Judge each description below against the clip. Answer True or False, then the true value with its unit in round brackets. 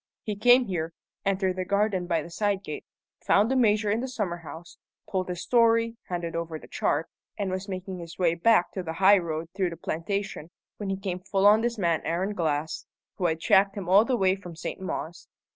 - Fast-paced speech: True (215 wpm)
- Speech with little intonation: False (3.3 semitones)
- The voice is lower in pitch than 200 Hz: True (190 Hz)